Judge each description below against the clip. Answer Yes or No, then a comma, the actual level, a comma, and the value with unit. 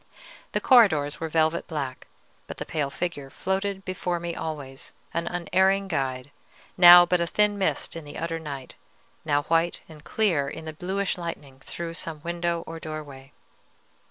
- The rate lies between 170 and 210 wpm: No, average, 160 wpm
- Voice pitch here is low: No, medium, 165 Hz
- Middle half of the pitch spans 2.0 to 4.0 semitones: Yes, average, 3.4 semitones